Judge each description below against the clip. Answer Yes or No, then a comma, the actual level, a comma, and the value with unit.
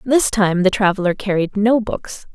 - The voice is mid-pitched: No, high, 205 Hz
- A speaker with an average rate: Yes, average, 180 wpm